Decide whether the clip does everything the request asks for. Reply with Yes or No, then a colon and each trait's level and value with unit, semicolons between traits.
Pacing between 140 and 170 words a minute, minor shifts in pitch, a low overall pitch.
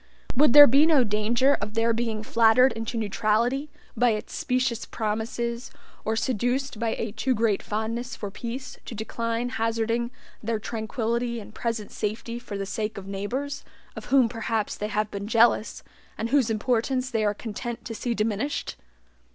No: average, 165 wpm; narrow, 2.3 semitones; high, 230 Hz